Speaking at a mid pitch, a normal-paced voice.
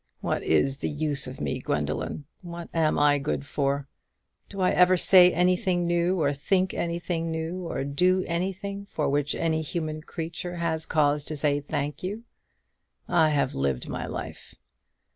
Yes: medium, 160 Hz; average, 160 wpm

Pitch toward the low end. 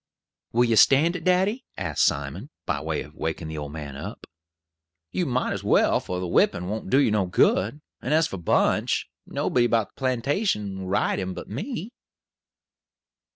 Yes: low, 110 Hz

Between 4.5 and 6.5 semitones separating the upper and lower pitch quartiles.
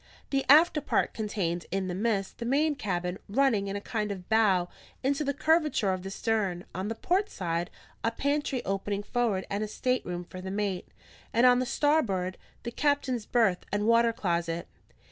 Yes: average, 5.2 semitones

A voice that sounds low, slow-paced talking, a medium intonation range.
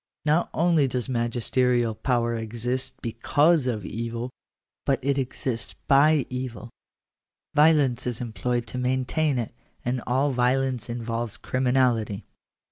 No: low, 125 Hz; slow, 120 wpm; narrow, 2.3 semitones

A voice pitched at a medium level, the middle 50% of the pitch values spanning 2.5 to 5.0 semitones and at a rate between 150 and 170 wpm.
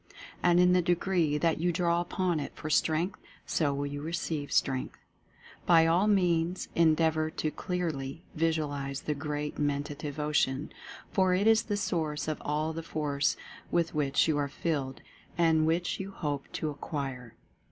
Yes: medium, 155 Hz; average, 3.0 semitones; average, 165 wpm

